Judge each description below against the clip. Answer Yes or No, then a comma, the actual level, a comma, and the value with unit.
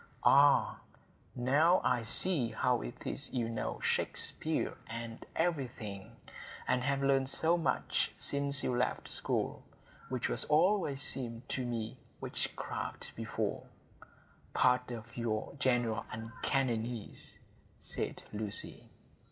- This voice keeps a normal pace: No, slow, 105 wpm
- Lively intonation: No, average, 3.4 semitones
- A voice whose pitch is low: Yes, low, 125 Hz